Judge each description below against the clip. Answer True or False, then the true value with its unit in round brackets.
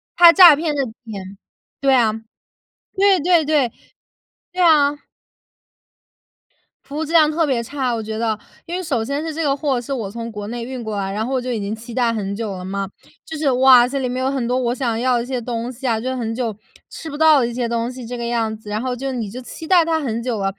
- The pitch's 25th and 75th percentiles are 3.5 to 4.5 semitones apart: True (3.9 semitones)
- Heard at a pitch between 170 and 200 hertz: False (250 Hz)